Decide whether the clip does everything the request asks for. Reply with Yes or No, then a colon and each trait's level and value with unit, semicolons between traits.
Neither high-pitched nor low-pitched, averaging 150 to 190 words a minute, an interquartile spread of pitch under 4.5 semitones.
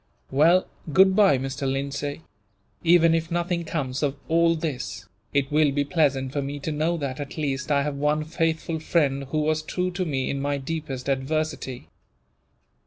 Yes: medium, 150 Hz; average, 170 wpm; average, 2.9 semitones